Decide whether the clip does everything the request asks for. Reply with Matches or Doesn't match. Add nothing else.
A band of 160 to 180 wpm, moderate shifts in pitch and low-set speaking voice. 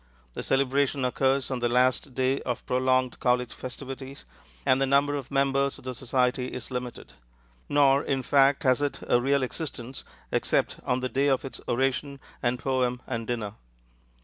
Doesn't match